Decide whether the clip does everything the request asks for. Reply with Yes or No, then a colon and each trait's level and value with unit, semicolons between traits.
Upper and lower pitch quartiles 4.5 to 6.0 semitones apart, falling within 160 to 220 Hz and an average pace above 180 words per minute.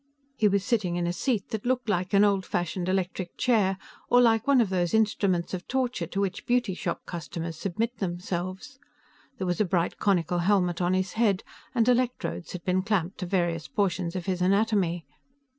No: average, 3.7 semitones; high, 190 Hz; average, 190 wpm